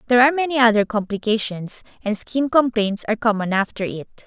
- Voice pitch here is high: Yes, high, 225 Hz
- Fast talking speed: No, average, 170 wpm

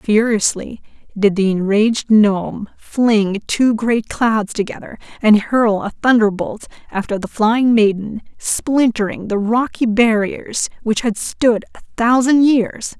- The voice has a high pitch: Yes, high, 220 Hz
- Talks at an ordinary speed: No, slow, 130 wpm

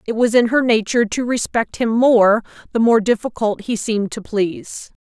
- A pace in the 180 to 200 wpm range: Yes, average, 190 wpm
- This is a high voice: Yes, high, 225 Hz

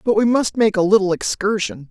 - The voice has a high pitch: Yes, high, 205 Hz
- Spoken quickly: Yes, fast, 220 wpm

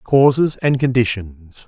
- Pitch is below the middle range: Yes, low, 120 Hz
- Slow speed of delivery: Yes, slow, 105 wpm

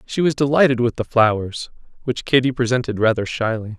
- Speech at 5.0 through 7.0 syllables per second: Yes, 5.7 syllables/s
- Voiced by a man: Yes, male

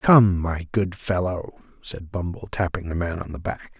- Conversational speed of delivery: Yes, average, 190 wpm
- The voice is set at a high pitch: No, very low, 90 Hz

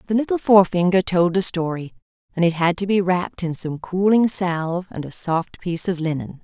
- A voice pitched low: No, medium, 180 Hz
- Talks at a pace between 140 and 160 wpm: No, fast, 205 wpm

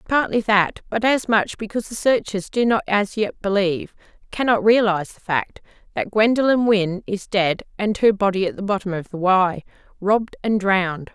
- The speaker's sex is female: Yes, female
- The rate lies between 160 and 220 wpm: Yes, average, 180 wpm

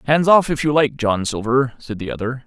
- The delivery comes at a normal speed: No, fast, 245 wpm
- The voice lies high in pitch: No, low, 130 Hz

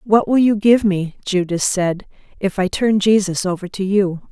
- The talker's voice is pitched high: Yes, high, 195 Hz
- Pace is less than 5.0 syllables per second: Yes, 4.6 syllables/s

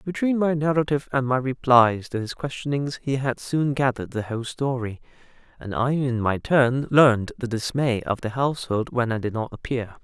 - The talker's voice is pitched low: Yes, low, 130 Hz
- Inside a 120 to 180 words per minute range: No, average, 190 wpm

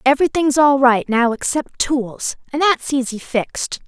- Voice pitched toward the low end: No, very high, 265 Hz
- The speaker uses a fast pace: No, average, 155 wpm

